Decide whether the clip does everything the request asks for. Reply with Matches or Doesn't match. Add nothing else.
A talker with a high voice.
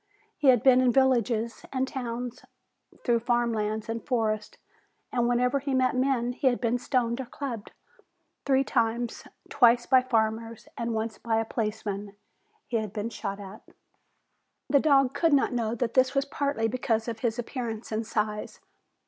Matches